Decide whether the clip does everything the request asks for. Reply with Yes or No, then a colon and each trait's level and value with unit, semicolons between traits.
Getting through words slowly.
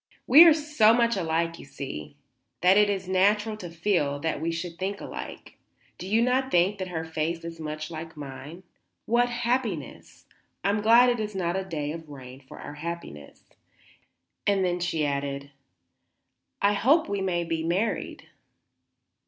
No: average, 170 wpm